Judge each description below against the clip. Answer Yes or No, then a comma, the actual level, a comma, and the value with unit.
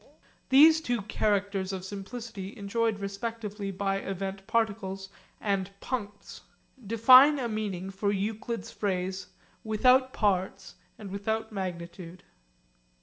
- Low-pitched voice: No, high, 200 Hz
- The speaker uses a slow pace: Yes, slow, 105 wpm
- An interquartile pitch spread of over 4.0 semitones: No, average, 2.8 semitones